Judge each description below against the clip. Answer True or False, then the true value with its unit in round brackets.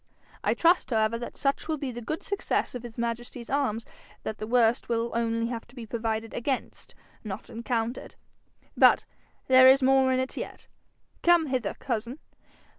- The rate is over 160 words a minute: True (170 wpm)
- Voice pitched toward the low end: False (240 Hz)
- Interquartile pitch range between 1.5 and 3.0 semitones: True (2.6 semitones)